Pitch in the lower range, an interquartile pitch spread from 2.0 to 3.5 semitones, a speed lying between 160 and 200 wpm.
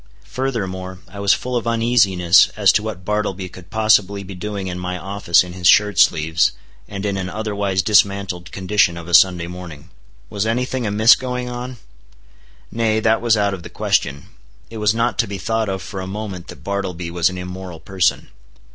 Yes: low, 100 Hz; average, 3.2 semitones; average, 190 wpm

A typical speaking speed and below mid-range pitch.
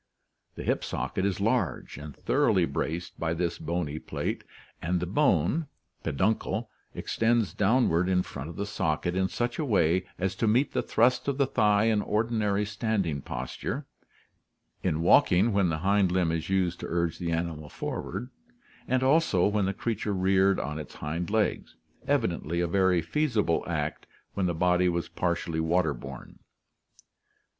Yes: average, 160 wpm; very low, 95 Hz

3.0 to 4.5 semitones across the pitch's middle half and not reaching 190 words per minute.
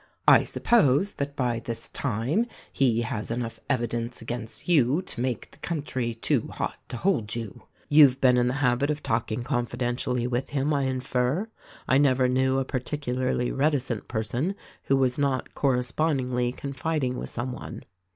No: narrow, 2.6 semitones; average, 170 wpm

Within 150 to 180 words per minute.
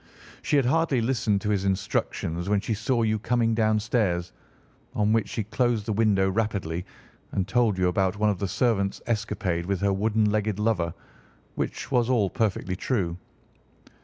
Yes: average, 165 wpm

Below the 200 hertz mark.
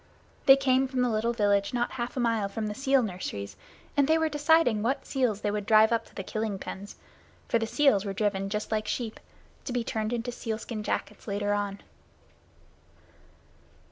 No: high, 220 Hz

